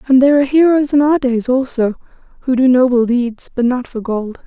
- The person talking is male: No, female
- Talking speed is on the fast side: Yes, fast, 215 wpm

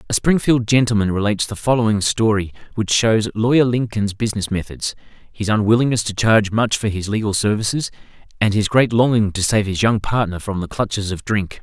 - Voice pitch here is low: Yes, low, 110 Hz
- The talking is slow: No, average, 185 wpm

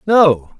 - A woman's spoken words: No, male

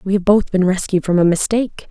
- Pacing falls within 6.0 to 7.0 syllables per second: Yes, 6.1 syllables/s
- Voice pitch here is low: No, high, 195 Hz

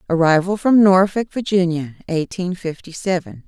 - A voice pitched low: No, medium, 180 Hz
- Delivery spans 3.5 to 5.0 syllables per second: Yes, 4.8 syllables/s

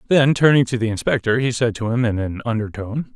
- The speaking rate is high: Yes, fast, 230 wpm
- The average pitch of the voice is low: Yes, low, 120 Hz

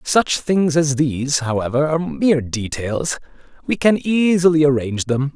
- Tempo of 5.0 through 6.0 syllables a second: No, 4.8 syllables/s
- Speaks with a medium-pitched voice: Yes, medium, 150 Hz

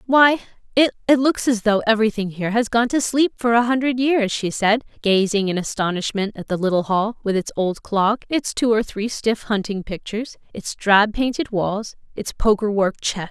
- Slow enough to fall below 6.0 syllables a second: Yes, 5.0 syllables/s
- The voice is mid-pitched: No, high, 220 Hz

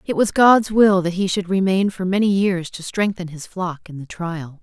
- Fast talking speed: Yes, fast, 235 wpm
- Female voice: Yes, female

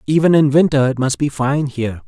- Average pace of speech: No, fast, 230 wpm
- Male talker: Yes, male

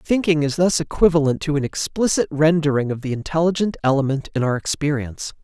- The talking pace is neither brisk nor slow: Yes, average, 165 wpm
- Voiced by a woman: No, male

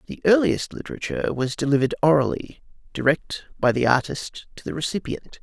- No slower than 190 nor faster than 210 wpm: No, average, 145 wpm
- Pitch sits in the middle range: Yes, medium, 145 Hz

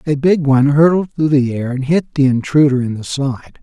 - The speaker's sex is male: Yes, male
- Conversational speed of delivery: No, fast, 230 wpm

